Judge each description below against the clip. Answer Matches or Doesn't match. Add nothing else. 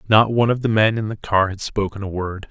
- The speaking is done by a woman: Doesn't match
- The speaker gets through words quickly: Matches